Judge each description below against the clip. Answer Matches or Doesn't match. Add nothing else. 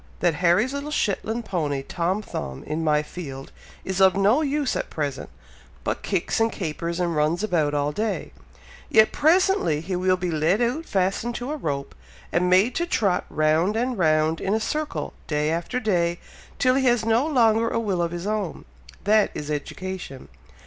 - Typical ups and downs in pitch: Doesn't match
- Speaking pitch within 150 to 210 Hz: Matches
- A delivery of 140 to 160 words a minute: Doesn't match